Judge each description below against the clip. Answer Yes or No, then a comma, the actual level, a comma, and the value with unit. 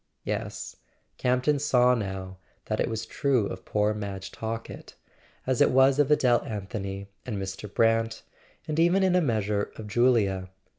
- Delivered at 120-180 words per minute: Yes, average, 155 wpm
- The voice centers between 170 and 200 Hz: No, low, 115 Hz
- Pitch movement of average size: Yes, average, 4.2 semitones